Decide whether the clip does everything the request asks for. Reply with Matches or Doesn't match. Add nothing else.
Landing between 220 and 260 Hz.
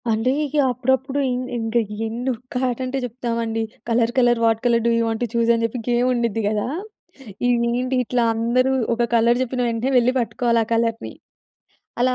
Matches